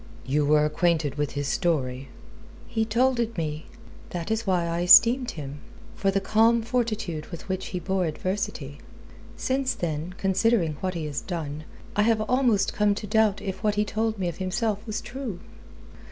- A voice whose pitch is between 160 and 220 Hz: Yes, high, 190 Hz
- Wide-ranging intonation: Yes, wide, 5.8 semitones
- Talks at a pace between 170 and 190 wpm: Yes, average, 175 wpm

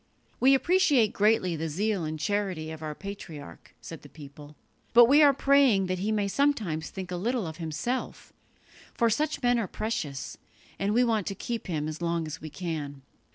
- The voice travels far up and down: Yes, wide, 6.8 semitones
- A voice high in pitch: Yes, high, 195 Hz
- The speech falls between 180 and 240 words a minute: Yes, average, 190 wpm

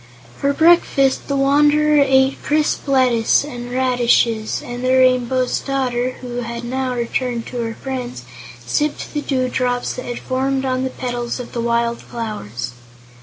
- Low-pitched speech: No, very high, 255 Hz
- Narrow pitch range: Yes, narrow, 1.9 semitones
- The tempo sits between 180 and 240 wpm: No, average, 150 wpm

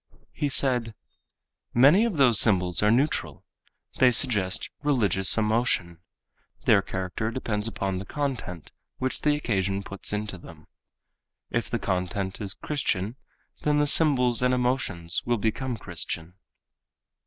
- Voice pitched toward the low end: Yes, low, 110 Hz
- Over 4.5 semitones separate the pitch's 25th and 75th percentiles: Yes, average, 5.2 semitones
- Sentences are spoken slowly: Yes, slow, 130 wpm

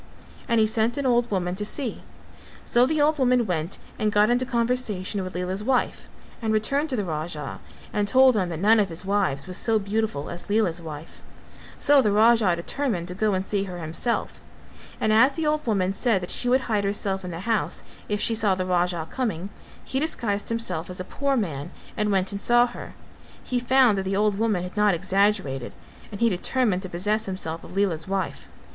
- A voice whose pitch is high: Yes, high, 205 Hz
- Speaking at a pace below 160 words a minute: No, fast, 205 wpm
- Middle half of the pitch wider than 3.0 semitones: Yes, average, 4.4 semitones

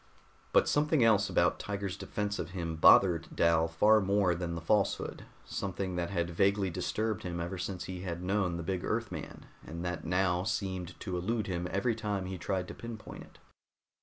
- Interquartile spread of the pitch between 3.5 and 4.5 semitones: No, average, 2.8 semitones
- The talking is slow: No, average, 185 wpm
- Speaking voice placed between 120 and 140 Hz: No, very low, 95 Hz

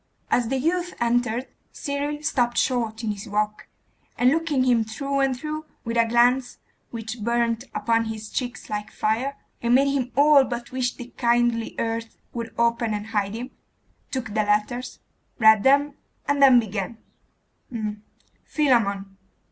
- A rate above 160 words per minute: No, average, 150 wpm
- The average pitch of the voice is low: No, high, 240 Hz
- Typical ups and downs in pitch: Yes, average, 3.2 semitones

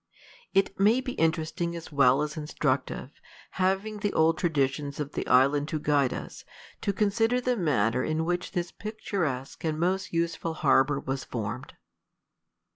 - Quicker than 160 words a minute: No, average, 150 wpm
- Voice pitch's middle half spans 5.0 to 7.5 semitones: Yes, average, 5.3 semitones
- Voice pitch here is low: No, medium, 160 Hz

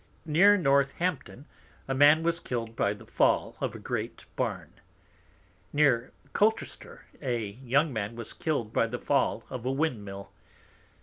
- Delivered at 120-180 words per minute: Yes, average, 145 wpm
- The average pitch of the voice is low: Yes, low, 130 Hz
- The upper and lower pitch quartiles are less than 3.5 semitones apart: No, average, 4.7 semitones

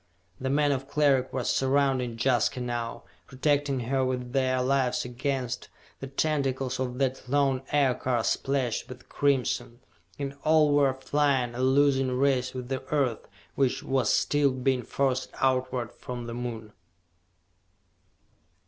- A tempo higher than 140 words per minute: No, slow, 135 wpm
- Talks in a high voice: No, low, 130 Hz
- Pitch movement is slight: Yes, narrow, 1.8 semitones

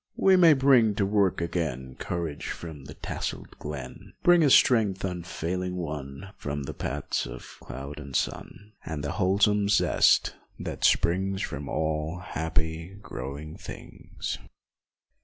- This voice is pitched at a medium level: No, very low, 85 Hz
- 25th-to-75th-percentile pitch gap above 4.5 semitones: Yes, average, 5.0 semitones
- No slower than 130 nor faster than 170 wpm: Yes, average, 140 wpm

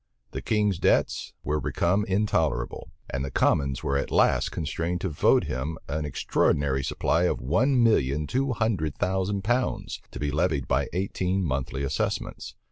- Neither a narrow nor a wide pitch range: No, wide, 6.0 semitones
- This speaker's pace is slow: No, average, 155 wpm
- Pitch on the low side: Yes, very low, 80 Hz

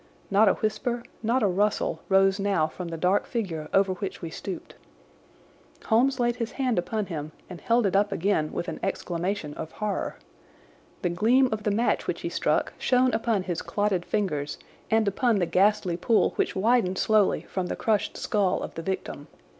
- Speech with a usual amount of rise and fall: Yes, average, 3.6 semitones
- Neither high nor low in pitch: No, high, 200 Hz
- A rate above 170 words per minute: Yes, average, 185 wpm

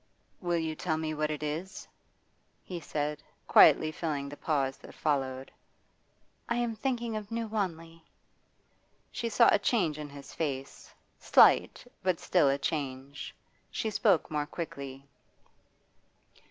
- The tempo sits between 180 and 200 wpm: No, slow, 135 wpm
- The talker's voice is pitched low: No, medium, 155 Hz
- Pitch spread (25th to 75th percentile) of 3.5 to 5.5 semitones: Yes, average, 4.8 semitones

